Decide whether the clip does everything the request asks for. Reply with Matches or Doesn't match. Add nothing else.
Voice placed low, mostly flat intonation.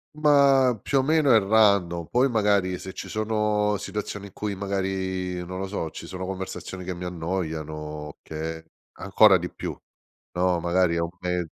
Doesn't match